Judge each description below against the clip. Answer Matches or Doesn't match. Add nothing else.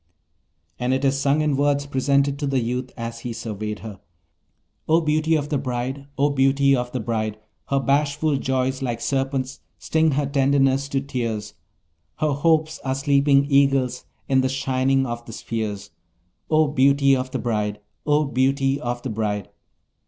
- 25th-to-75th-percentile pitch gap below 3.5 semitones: Matches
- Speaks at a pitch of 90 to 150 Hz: Matches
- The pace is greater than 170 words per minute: Doesn't match